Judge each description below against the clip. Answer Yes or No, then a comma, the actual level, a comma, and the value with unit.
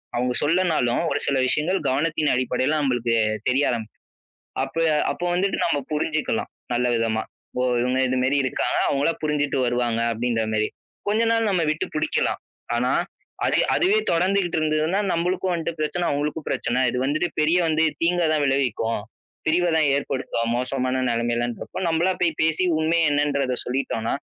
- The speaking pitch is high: No, medium, 145 Hz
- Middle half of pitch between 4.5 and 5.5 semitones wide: Yes, average, 4.8 semitones